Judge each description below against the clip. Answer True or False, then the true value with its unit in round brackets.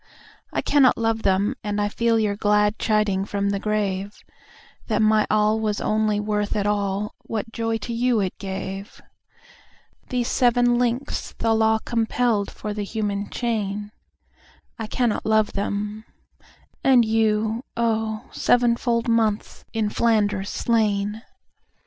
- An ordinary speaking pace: False (120 wpm)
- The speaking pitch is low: False (215 Hz)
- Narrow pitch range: True (1.9 semitones)